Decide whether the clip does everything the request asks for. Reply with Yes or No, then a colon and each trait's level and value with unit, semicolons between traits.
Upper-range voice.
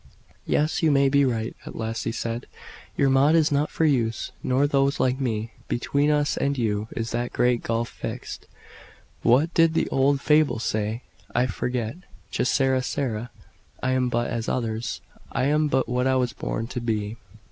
No: low, 125 Hz